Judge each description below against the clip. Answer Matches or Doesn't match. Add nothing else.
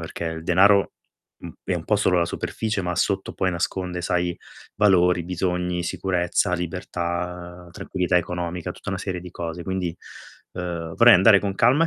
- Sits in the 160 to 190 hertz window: Doesn't match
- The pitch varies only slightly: Matches